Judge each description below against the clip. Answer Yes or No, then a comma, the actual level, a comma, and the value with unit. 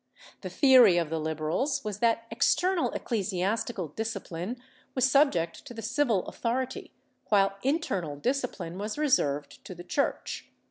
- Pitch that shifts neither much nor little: No, wide, 6.8 semitones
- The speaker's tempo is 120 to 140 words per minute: Yes, slow, 135 wpm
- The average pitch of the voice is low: No, high, 220 Hz